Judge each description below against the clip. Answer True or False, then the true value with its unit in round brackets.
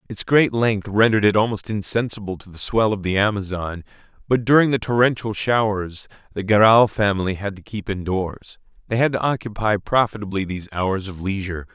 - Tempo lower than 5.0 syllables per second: False (5.5 syllables/s)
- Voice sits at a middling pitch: False (105 Hz)